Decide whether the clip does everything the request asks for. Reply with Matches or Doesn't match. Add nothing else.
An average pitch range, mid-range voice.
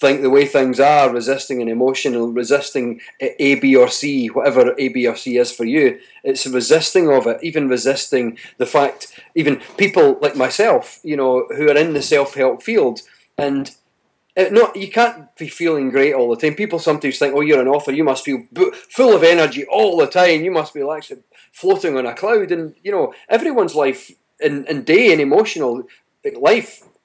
Doesn't match